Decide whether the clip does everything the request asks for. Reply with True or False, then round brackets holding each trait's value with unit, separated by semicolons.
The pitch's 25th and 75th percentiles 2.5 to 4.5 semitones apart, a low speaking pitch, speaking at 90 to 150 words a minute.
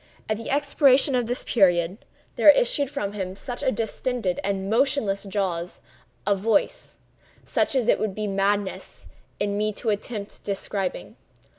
False (4.0 semitones; 210 Hz; 135 wpm)